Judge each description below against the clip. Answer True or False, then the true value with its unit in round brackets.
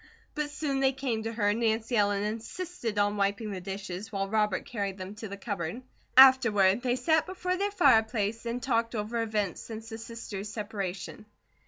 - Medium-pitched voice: False (220 Hz)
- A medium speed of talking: True (180 wpm)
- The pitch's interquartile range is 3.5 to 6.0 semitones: False (3.1 semitones)